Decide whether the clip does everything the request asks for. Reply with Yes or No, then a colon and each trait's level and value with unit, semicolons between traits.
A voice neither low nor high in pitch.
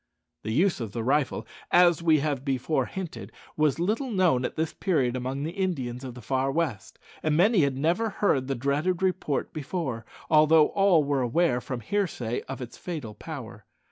Yes: medium, 150 Hz